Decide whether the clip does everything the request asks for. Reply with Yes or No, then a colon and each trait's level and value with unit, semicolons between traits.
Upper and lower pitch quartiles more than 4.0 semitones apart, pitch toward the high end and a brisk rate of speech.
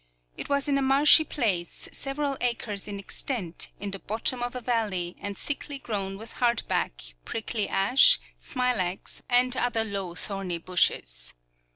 No: average, 4.7 semitones; high, 225 Hz; average, 150 wpm